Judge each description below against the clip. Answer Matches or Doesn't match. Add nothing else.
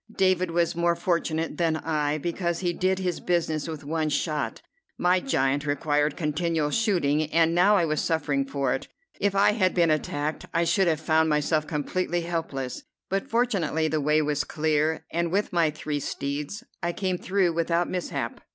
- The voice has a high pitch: Doesn't match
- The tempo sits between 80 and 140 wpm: Doesn't match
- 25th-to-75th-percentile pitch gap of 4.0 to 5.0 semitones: Doesn't match